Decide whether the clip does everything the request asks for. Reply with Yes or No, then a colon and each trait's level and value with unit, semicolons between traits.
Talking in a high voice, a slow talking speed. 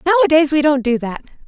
No: very high, 295 Hz; fast, 205 wpm